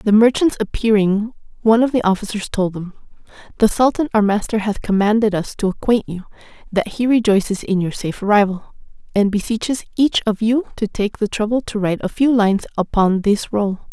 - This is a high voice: Yes, high, 215 Hz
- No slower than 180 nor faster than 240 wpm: Yes, average, 185 wpm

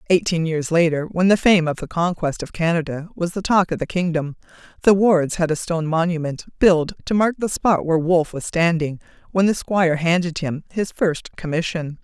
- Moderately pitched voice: Yes, medium, 170 Hz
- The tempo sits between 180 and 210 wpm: Yes, average, 200 wpm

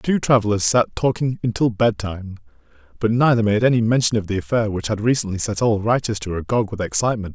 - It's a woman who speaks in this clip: No, male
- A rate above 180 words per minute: Yes, average, 190 wpm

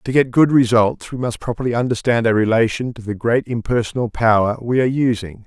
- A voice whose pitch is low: Yes, low, 115 Hz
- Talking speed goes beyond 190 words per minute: Yes, average, 200 wpm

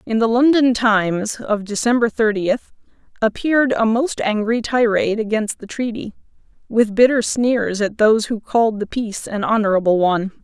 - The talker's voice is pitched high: Yes, high, 220 Hz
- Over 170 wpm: No, average, 155 wpm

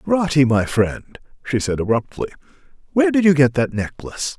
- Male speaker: Yes, male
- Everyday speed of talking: Yes, average, 165 wpm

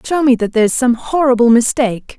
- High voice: Yes, high, 245 Hz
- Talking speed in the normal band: Yes, average, 190 wpm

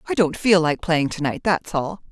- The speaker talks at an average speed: No, fast, 255 wpm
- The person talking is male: No, female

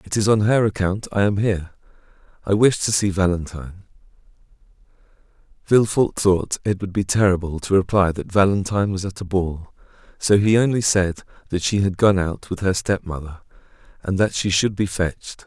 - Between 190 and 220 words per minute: No, average, 180 wpm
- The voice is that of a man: Yes, male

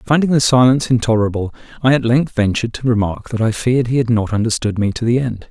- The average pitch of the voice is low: Yes, low, 120 Hz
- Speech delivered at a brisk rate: Yes, fast, 230 wpm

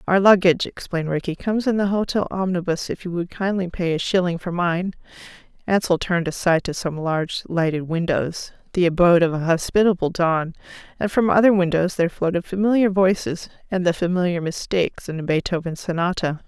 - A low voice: No, medium, 175 Hz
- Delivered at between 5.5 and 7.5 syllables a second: Yes, 5.9 syllables/s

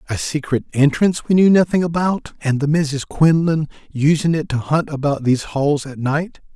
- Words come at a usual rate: Yes, average, 185 wpm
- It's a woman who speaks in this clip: No, male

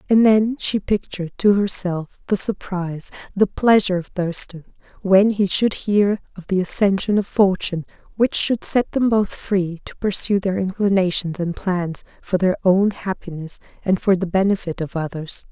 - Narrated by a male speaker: No, female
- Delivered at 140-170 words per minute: Yes, average, 165 wpm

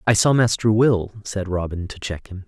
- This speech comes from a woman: No, male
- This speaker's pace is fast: Yes, fast, 220 wpm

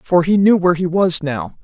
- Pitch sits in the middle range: Yes, medium, 180 Hz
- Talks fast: Yes, fast, 255 wpm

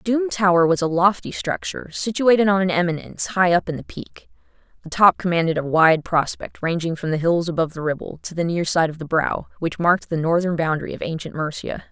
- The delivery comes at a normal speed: No, fast, 215 wpm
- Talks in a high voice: No, medium, 175 Hz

